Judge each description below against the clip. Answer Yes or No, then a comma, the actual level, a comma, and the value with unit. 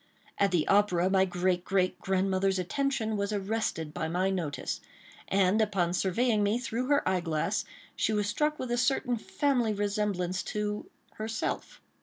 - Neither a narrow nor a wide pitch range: Yes, average, 3.2 semitones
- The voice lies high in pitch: Yes, high, 200 Hz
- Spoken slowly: No, average, 155 wpm